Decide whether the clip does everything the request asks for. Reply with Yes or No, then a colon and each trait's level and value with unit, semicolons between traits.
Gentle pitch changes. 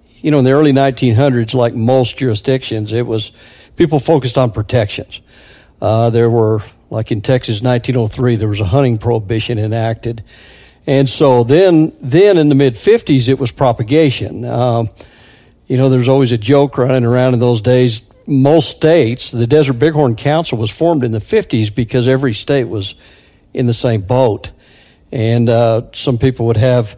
No: average, 3.0 semitones